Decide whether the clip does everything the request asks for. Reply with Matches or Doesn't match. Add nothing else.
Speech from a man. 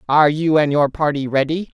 Doesn't match